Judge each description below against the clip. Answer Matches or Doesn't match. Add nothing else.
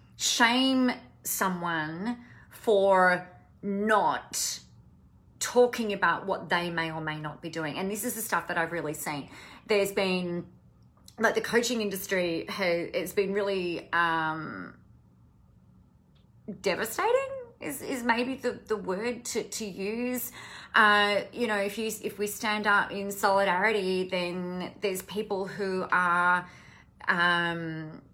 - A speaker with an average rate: Doesn't match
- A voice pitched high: Matches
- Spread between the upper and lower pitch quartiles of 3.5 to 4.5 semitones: Matches